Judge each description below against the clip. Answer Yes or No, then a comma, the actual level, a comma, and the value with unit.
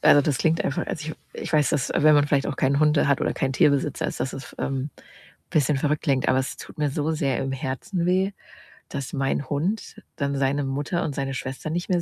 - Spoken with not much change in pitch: Yes, narrow, 2.3 semitones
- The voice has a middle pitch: Yes, medium, 145 Hz